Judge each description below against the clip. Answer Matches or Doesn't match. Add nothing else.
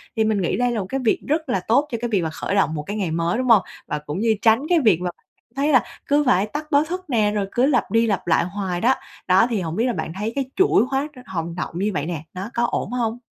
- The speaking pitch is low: Doesn't match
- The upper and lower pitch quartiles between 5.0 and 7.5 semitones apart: Matches